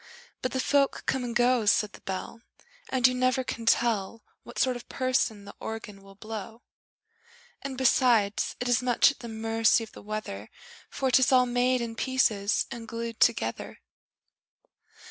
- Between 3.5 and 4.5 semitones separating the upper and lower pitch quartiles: No, average, 2.8 semitones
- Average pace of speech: Yes, average, 165 wpm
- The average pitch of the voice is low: No, high, 235 Hz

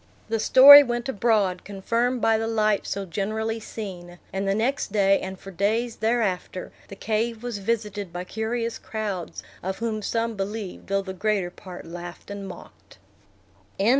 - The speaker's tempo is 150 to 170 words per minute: Yes, average, 160 wpm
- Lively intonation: No, average, 2.8 semitones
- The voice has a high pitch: Yes, high, 210 Hz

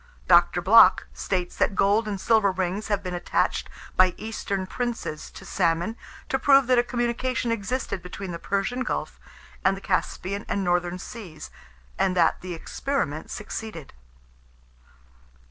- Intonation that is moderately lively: Yes, average, 4.1 semitones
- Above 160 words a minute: No, average, 145 wpm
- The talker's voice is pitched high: Yes, high, 195 Hz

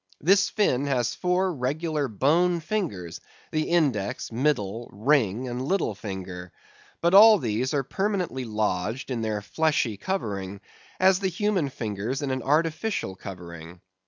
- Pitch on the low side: Yes, low, 130 Hz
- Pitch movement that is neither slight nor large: No, wide, 8.5 semitones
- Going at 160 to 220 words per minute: No, slow, 135 wpm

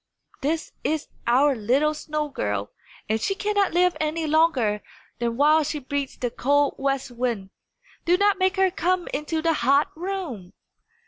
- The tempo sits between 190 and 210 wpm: No, average, 155 wpm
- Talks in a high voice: Yes, very high, 295 Hz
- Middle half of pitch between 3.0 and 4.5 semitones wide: No, average, 5.1 semitones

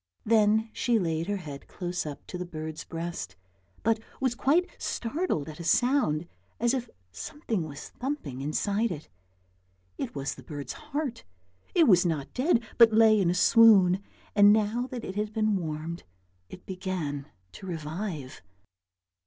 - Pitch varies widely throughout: Yes, wide, 6.4 semitones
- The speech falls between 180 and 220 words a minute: No, average, 155 wpm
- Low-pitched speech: No, high, 190 Hz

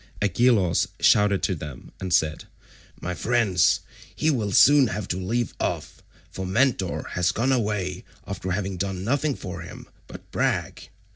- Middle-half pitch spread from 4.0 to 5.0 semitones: Yes, average, 4.6 semitones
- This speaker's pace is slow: No, average, 150 wpm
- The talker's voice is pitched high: No, low, 100 Hz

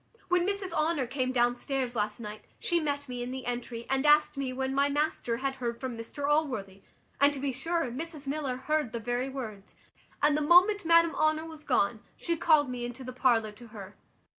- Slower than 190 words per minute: No, fast, 205 wpm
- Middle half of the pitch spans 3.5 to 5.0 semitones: Yes, average, 4.0 semitones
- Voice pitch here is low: No, very high, 265 Hz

